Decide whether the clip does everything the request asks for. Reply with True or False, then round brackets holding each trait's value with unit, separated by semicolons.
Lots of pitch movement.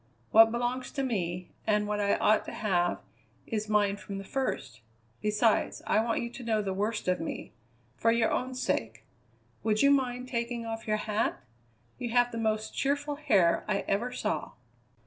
False (3.1 semitones)